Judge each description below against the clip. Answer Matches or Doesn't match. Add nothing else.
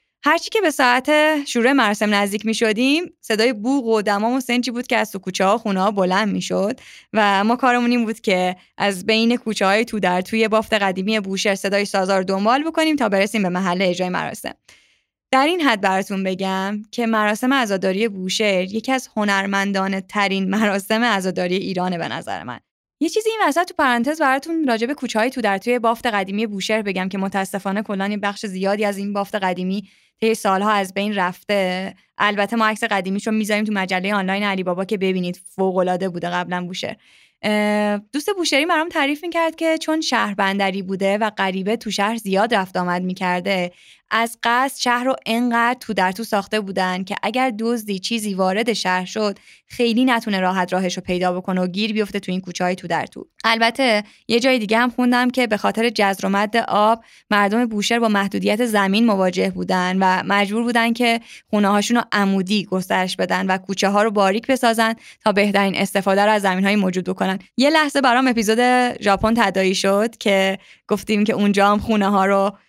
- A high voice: Matches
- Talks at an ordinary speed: Doesn't match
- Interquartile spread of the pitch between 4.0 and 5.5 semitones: Doesn't match